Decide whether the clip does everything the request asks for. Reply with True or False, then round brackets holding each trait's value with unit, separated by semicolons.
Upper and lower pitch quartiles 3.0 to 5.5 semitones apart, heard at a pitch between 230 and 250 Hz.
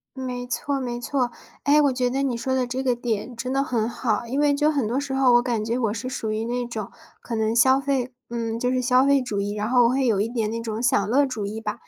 False (2.5 semitones; 245 Hz)